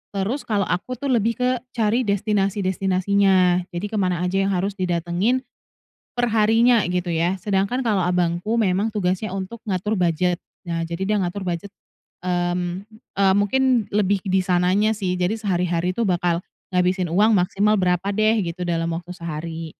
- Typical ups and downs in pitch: Yes, average, 3.0 semitones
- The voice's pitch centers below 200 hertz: Yes, high, 190 Hz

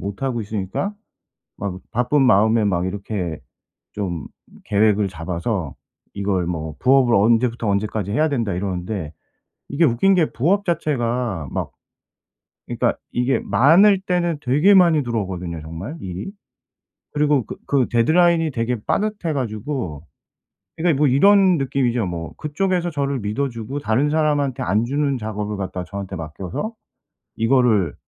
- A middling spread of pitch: No, wide, 7.0 semitones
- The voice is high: No, low, 120 Hz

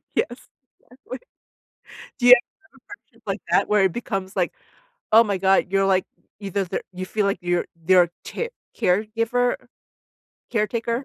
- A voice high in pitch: Yes, high, 200 Hz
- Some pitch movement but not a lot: Yes, average, 4.0 semitones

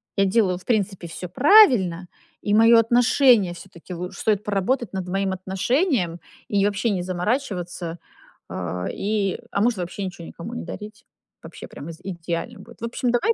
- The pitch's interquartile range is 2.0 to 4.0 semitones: No, average, 4.4 semitones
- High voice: Yes, high, 195 Hz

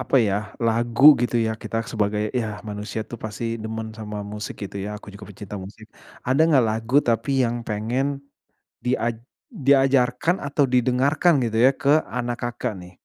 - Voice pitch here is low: Yes, low, 120 Hz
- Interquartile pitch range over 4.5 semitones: No, average, 3.6 semitones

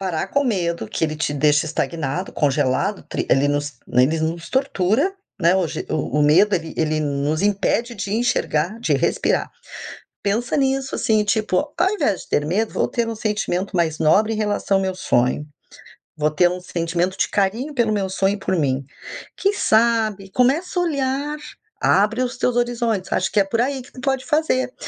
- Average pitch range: No, wide, 6.8 semitones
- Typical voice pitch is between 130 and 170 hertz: No, high, 195 Hz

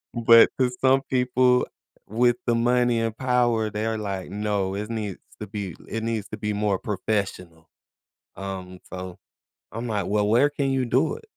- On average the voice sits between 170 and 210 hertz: No, low, 110 Hz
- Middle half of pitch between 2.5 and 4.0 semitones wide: Yes, average, 3.4 semitones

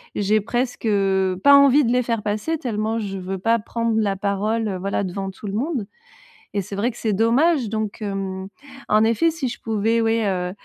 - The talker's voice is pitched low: No, high, 215 Hz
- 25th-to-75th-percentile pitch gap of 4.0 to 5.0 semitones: No, average, 2.8 semitones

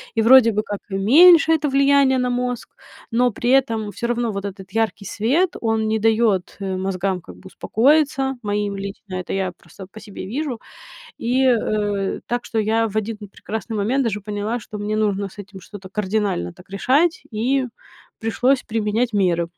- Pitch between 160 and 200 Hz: No, high, 220 Hz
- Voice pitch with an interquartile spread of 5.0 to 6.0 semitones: No, average, 3.7 semitones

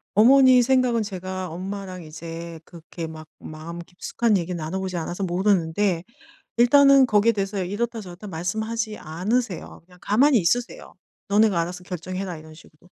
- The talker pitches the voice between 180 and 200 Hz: Yes, medium, 185 Hz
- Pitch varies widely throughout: No, average, 4.4 semitones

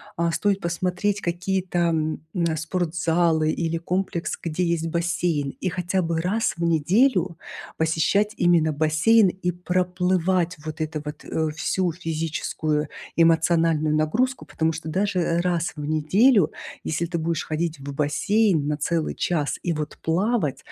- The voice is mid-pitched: Yes, medium, 170 Hz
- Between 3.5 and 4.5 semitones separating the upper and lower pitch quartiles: No, narrow, 2.5 semitones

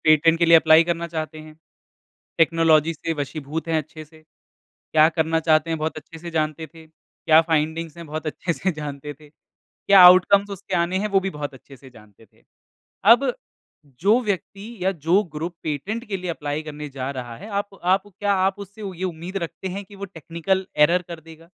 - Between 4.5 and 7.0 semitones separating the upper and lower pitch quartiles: No, average, 3.3 semitones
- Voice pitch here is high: No, medium, 165 Hz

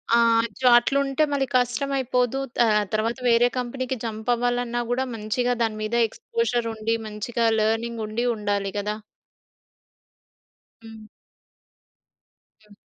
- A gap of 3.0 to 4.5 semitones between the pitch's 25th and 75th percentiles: No, narrow, 2.4 semitones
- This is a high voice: Yes, high, 235 Hz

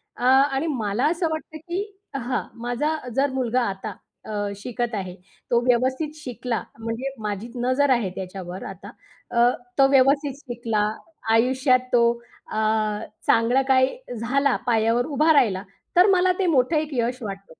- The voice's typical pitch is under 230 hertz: No, very high, 250 Hz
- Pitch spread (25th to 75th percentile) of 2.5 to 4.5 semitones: Yes, average, 3.5 semitones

